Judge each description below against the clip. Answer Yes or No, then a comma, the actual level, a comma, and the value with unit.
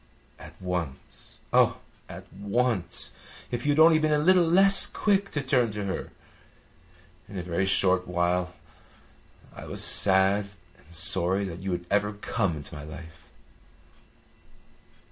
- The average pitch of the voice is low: Yes, very low, 95 Hz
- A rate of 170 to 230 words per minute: No, average, 145 wpm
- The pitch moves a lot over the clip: Yes, wide, 6.4 semitones